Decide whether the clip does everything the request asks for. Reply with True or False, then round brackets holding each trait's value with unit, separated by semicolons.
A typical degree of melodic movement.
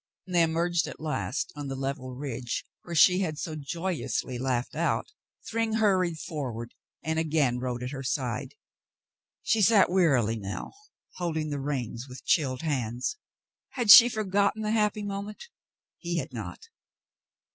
False (6.4 semitones)